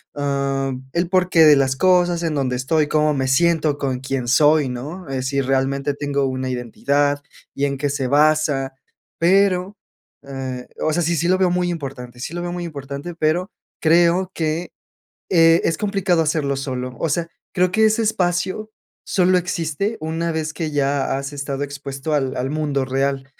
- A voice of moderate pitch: Yes, medium, 150 Hz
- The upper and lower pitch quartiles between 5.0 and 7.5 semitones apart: No, average, 4.0 semitones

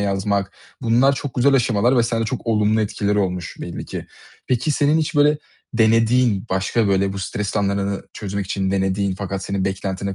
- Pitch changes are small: No, average, 3.5 semitones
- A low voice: Yes, low, 105 Hz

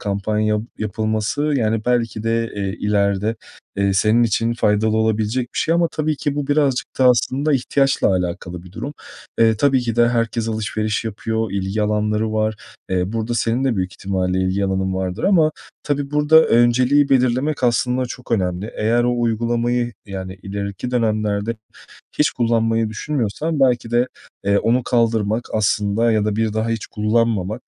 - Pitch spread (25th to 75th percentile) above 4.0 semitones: No, average, 2.9 semitones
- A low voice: Yes, low, 115 Hz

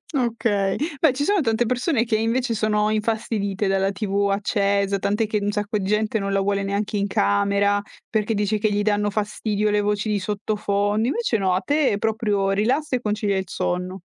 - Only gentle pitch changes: Yes, narrow, 1.8 semitones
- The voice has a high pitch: Yes, high, 210 Hz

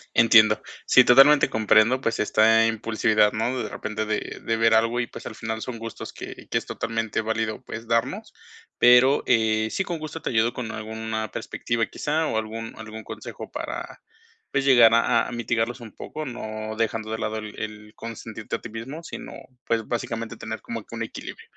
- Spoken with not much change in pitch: Yes, narrow, 1.3 semitones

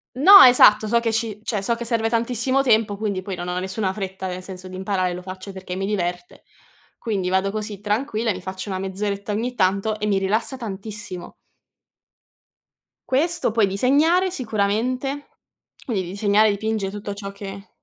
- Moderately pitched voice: No, high, 205 Hz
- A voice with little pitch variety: No, average, 3.2 semitones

